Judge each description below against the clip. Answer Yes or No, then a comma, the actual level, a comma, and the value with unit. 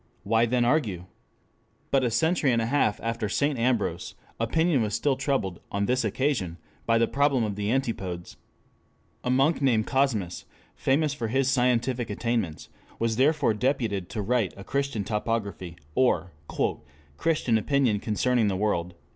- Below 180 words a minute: Yes, average, 150 wpm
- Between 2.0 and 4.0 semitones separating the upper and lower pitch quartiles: No, average, 4.4 semitones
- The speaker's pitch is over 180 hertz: No, low, 115 Hz